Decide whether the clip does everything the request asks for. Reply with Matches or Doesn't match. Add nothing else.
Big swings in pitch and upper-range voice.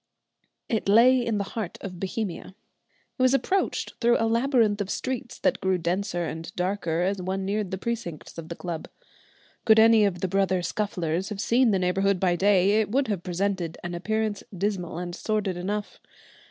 Doesn't match